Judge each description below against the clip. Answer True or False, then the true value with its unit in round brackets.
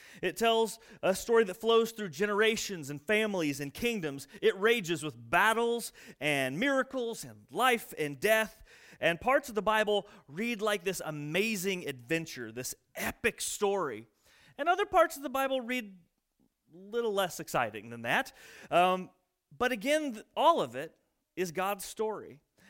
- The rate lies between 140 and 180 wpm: True (150 wpm)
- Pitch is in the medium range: False (205 Hz)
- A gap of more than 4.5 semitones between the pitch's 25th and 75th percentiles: True (5.2 semitones)